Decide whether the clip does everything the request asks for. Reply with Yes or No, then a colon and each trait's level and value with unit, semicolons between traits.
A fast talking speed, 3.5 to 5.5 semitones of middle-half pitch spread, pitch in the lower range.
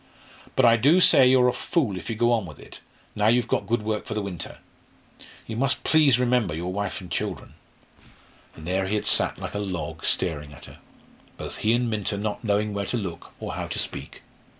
Yes: fast, 220 wpm; average, 4.2 semitones; low, 105 Hz